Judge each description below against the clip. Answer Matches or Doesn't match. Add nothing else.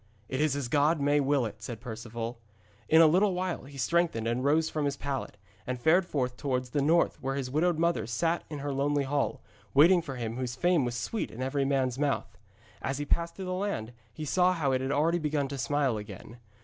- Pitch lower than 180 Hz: Matches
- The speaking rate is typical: Doesn't match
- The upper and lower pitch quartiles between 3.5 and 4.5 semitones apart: Matches